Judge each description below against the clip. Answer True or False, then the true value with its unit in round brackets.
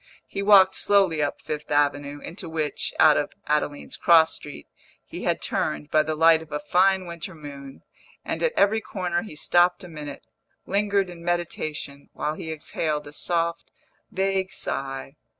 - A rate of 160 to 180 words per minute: True (165 wpm)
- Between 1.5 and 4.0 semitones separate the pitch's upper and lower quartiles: True (3.7 semitones)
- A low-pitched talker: False (160 Hz)